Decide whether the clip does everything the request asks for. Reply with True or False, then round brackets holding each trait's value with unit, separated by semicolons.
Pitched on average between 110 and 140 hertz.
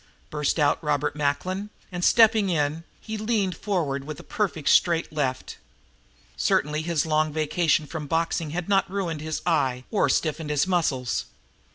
False (160 Hz)